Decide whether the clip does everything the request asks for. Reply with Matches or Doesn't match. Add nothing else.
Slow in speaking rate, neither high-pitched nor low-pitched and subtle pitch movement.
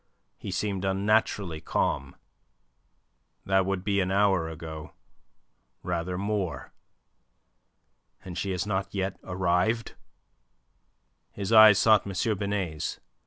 Doesn't match